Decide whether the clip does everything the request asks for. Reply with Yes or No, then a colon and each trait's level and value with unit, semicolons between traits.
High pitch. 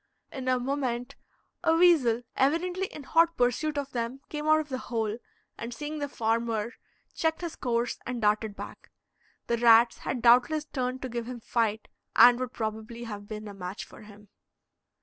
Yes: high, 245 Hz